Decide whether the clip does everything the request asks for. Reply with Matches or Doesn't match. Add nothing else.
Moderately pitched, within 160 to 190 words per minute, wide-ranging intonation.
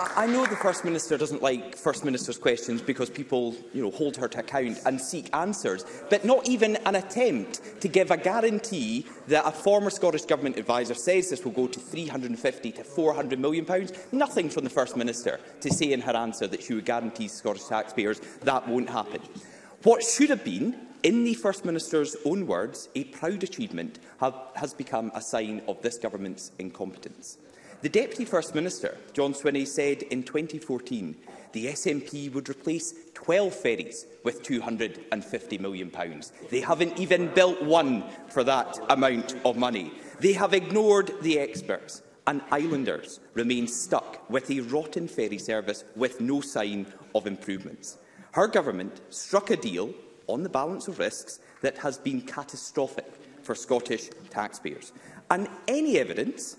Matches